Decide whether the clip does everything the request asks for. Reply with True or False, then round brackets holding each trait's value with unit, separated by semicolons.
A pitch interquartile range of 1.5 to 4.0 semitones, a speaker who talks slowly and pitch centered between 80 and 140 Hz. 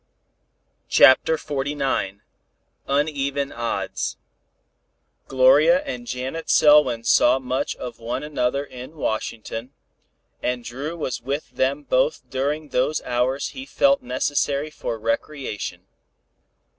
True (3.3 semitones; 105 wpm; 135 Hz)